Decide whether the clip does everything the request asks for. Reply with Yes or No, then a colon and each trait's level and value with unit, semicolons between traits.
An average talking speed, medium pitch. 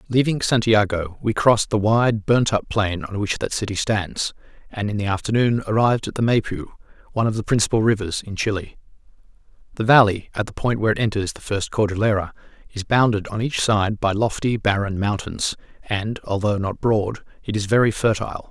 No: average, 185 wpm; low, 105 Hz